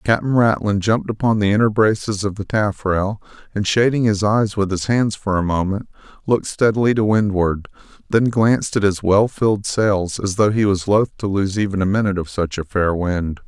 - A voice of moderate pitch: No, low, 105 Hz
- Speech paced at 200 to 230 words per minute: Yes, fast, 205 wpm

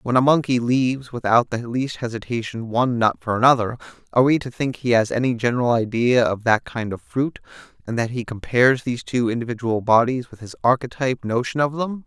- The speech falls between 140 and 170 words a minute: No, average, 200 wpm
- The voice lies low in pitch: Yes, low, 120 Hz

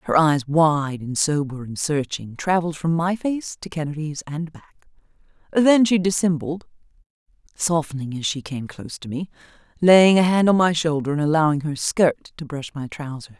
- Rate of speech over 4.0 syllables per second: Yes, 5.1 syllables/s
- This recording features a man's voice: No, female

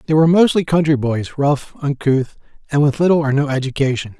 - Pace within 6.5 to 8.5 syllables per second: No, 5.8 syllables/s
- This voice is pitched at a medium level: Yes, medium, 145 Hz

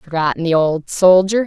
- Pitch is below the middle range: No, medium, 175 Hz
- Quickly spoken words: No, average, 165 wpm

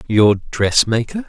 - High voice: No, low, 120 Hz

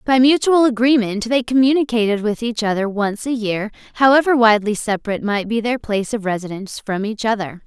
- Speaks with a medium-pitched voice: No, high, 225 Hz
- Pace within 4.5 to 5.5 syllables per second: No, 6.0 syllables/s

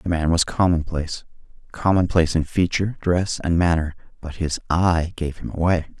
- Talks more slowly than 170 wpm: Yes, average, 150 wpm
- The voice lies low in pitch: Yes, very low, 85 Hz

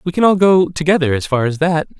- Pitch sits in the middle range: Yes, medium, 165 Hz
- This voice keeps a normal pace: No, fast, 270 wpm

